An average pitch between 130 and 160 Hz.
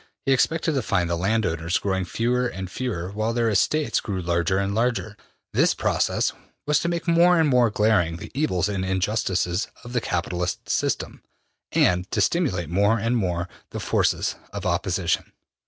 No: low, 105 Hz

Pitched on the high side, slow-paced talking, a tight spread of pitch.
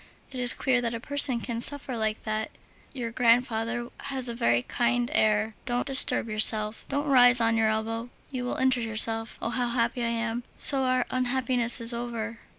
No: high, 235 Hz; average, 185 wpm; narrow, 1.9 semitones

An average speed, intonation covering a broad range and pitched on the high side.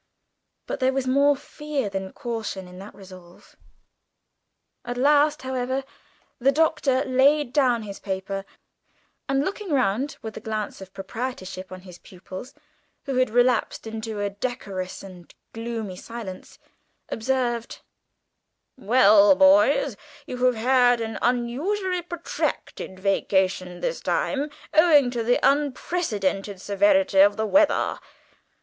No: slow, 125 wpm; wide, 5.8 semitones; high, 240 Hz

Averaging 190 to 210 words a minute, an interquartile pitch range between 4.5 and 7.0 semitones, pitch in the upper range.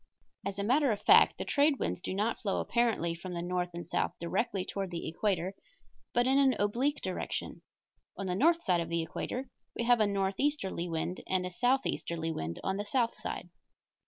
Yes: average, 195 wpm; wide, 5.6 semitones; high, 200 Hz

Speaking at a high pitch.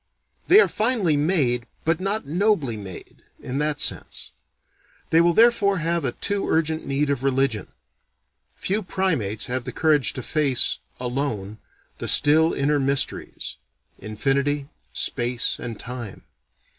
No: medium, 145 Hz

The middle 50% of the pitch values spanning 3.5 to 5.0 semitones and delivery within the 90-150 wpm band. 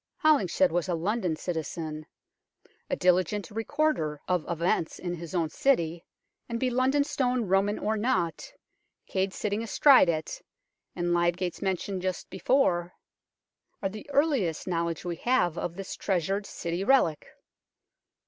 Yes: average, 4.7 semitones; average, 140 wpm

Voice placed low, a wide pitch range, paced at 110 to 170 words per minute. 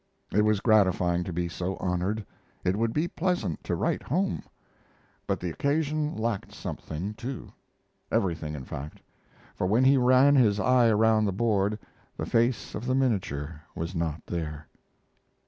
Yes: low, 105 Hz; wide, 6.1 semitones; average, 155 wpm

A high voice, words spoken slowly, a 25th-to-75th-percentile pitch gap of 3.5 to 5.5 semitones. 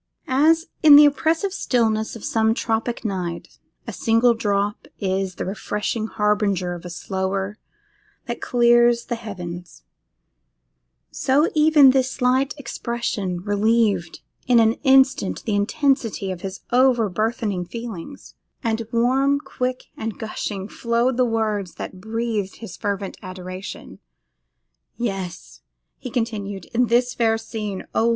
Yes: high, 225 Hz; slow, 130 wpm; average, 3.8 semitones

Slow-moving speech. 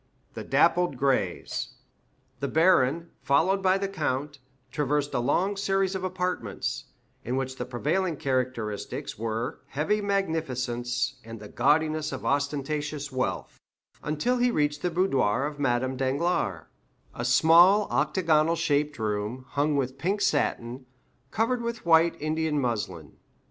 Yes: slow, 130 wpm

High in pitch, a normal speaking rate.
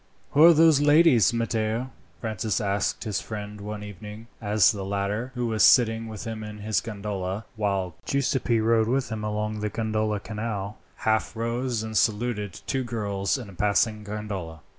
No: low, 110 Hz; average, 160 wpm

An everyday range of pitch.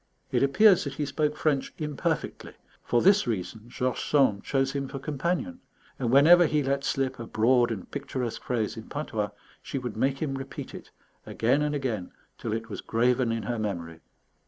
Yes: average, 4.1 semitones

